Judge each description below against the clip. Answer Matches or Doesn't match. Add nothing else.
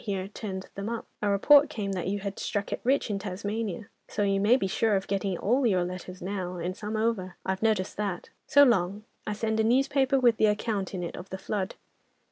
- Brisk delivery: Matches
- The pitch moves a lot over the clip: Doesn't match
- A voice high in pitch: Matches